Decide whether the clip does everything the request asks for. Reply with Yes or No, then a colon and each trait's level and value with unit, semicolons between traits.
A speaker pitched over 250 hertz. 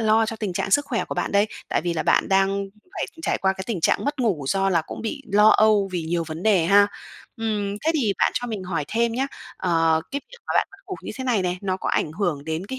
No: high, 200 Hz